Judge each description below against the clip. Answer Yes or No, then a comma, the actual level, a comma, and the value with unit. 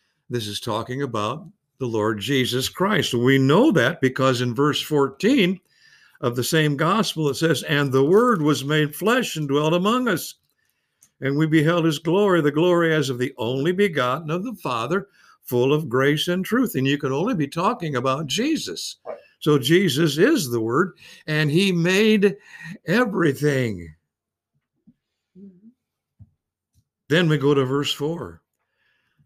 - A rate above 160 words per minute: No, average, 150 wpm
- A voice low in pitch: No, medium, 155 Hz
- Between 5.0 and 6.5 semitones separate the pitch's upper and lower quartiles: Yes, average, 5.3 semitones